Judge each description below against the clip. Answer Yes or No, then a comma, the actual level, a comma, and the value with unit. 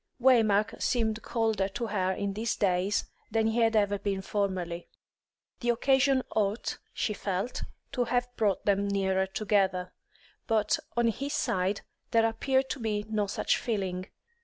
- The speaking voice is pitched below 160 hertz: No, high, 210 Hz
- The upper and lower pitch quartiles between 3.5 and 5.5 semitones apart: No, average, 3.0 semitones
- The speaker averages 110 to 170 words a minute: Yes, average, 150 wpm